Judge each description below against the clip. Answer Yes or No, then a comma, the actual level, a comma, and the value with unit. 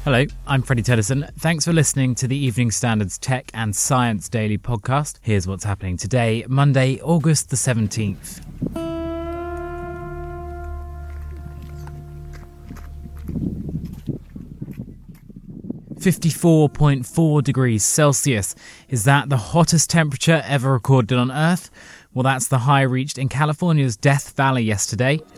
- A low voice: Yes, low, 125 Hz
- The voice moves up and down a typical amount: No, wide, 7.5 semitones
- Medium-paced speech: No, slow, 110 wpm